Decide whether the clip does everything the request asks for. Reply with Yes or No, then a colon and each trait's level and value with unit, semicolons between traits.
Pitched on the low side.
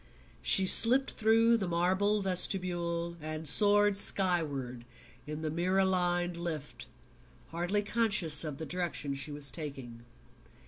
No: medium, 175 Hz